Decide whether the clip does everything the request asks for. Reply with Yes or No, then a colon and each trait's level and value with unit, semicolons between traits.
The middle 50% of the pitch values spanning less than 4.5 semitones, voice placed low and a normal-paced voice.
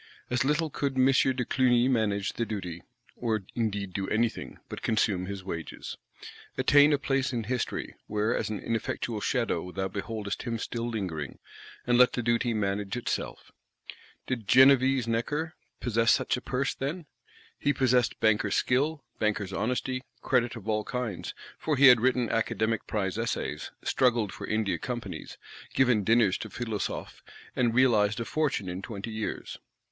Yes: average, 3.5 semitones; low, 115 Hz; average, 155 wpm